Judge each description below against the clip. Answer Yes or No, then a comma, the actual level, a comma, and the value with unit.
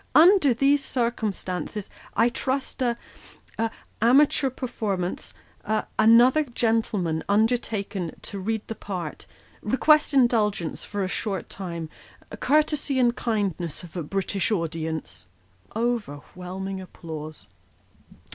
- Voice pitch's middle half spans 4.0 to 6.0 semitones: Yes, average, 5.1 semitones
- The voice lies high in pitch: Yes, high, 215 Hz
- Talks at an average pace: No, slow, 105 wpm